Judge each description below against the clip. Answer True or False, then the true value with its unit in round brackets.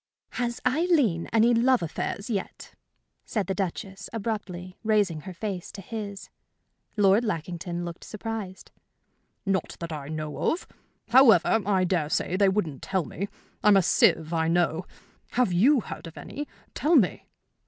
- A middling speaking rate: True (150 wpm)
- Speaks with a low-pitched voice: False (195 Hz)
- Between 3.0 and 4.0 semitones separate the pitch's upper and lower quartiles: False (4.5 semitones)